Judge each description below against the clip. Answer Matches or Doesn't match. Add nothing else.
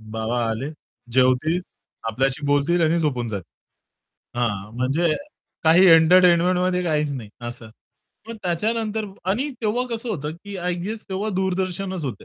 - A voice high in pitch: Doesn't match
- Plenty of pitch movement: Matches